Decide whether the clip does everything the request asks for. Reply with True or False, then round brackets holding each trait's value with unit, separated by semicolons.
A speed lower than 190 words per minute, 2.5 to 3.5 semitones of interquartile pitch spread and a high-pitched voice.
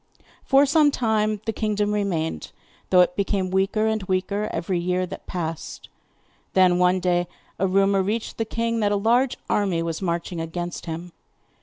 True (165 wpm; 3.2 semitones; 195 Hz)